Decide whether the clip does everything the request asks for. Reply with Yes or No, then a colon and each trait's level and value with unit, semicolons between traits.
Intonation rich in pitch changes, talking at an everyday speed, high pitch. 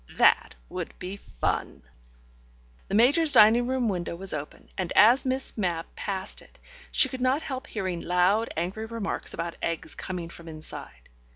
Yes: wide, 5.9 semitones; average, 160 wpm; high, 195 Hz